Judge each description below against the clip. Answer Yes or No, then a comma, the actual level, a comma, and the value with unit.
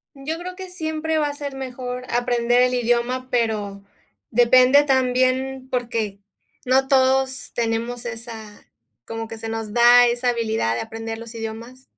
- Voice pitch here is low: No, high, 245 Hz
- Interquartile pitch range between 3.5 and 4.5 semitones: No, narrow, 2.6 semitones